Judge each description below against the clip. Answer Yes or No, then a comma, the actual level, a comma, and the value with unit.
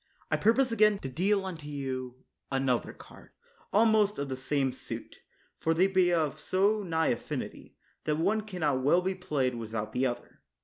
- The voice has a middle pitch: Yes, medium, 160 Hz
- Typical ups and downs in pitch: No, wide, 6.8 semitones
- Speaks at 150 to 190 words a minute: Yes, average, 180 wpm